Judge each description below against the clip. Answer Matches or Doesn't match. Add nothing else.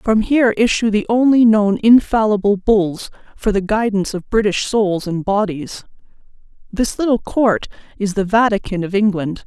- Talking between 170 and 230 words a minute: Doesn't match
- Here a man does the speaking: Doesn't match